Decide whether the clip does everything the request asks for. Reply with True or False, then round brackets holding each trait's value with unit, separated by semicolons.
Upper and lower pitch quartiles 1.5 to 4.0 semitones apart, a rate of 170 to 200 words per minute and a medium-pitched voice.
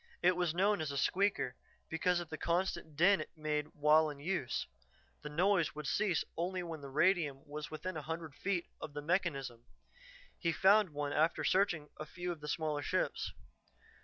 True (3.4 semitones; 180 wpm; 160 Hz)